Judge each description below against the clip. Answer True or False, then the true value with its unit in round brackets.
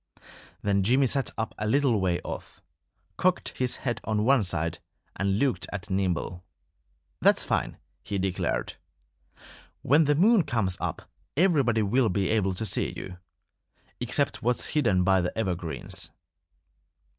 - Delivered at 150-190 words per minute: False (140 wpm)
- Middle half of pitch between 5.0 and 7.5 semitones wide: True (5.6 semitones)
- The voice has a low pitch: True (105 Hz)